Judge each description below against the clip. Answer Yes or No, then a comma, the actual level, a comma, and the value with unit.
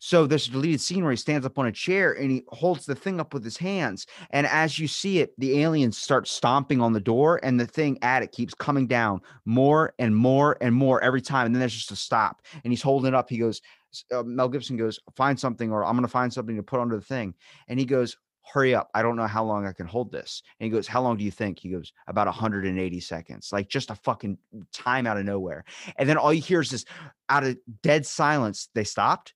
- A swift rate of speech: Yes, fast, 260 wpm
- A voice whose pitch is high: No, low, 125 Hz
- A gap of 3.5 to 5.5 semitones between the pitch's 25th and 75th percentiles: Yes, average, 4.3 semitones